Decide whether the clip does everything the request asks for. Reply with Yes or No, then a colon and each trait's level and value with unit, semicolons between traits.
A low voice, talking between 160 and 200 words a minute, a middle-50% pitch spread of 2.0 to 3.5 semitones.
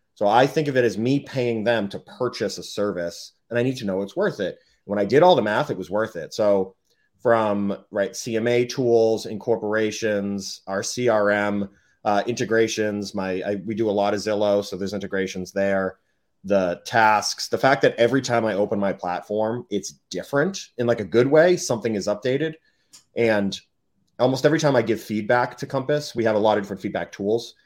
Yes: low, 110 Hz; average, 195 wpm; average, 3.1 semitones